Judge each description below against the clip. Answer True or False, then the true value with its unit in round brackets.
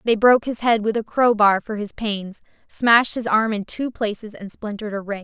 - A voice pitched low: False (215 Hz)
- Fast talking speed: True (230 wpm)